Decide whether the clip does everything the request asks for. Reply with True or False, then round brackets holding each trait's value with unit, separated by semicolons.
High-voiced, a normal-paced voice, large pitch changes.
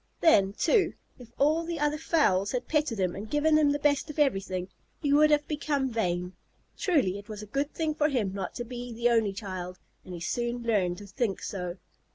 False (240 Hz; 210 wpm; 7.2 semitones)